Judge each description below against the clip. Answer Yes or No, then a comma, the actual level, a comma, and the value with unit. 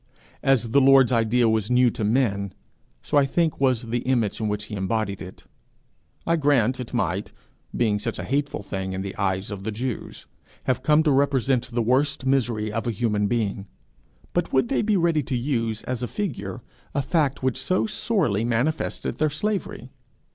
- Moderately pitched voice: No, low, 120 Hz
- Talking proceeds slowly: No, average, 185 wpm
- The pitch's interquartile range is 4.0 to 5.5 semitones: Yes, average, 4.3 semitones